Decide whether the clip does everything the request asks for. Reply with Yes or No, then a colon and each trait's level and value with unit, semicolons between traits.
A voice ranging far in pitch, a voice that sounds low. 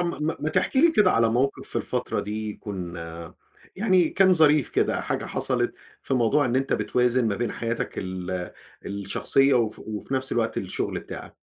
Yes: wide, 6.1 semitones; low, 120 Hz